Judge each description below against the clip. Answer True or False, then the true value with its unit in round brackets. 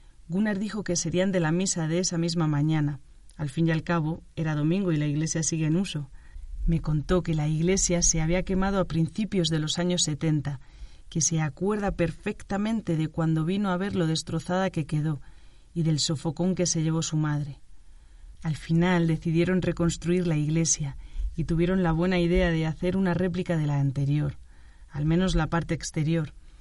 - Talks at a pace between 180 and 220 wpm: True (185 wpm)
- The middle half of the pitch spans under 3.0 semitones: True (2.5 semitones)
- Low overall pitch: False (165 Hz)